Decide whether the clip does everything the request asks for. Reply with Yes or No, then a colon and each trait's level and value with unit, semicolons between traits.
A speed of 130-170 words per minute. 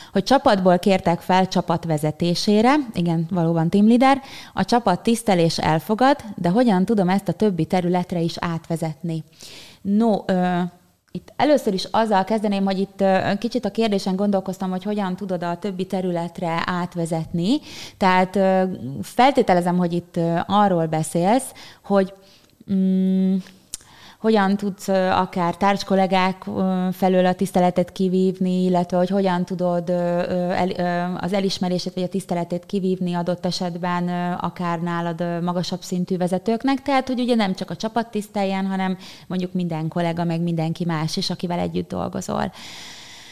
Yes: average, 135 wpm